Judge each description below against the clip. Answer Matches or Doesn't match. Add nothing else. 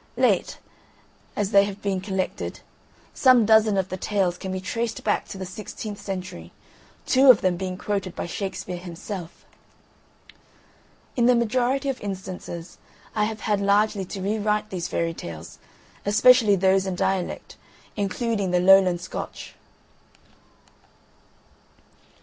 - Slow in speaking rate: Matches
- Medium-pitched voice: Doesn't match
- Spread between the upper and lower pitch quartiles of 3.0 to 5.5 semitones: Doesn't match